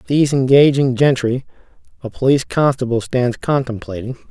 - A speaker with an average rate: No, slow, 110 wpm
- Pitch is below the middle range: Yes, low, 130 Hz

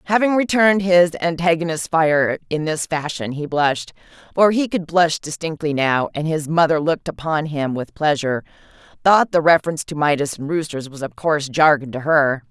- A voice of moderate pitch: Yes, medium, 160 Hz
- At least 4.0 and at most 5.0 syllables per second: No, 5.3 syllables/s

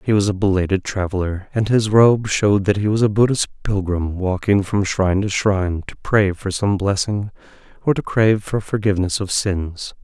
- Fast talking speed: No, average, 190 wpm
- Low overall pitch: Yes, low, 100 Hz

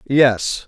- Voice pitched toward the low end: Yes, low, 130 Hz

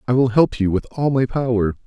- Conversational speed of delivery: No, fast, 260 wpm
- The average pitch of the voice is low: Yes, low, 120 Hz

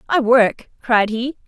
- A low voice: No, high, 240 Hz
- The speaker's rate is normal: Yes, average, 165 wpm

